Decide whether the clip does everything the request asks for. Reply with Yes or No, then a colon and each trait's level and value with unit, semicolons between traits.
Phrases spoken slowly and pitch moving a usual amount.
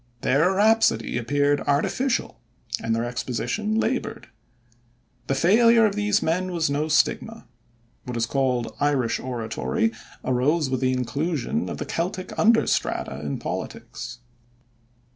No: slow, 125 wpm; wide, 8.5 semitones